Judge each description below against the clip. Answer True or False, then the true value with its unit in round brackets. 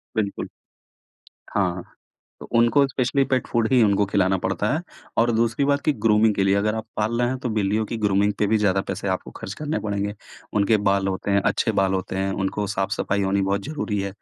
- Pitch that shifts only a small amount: False (3.0 semitones)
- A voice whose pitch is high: False (105 Hz)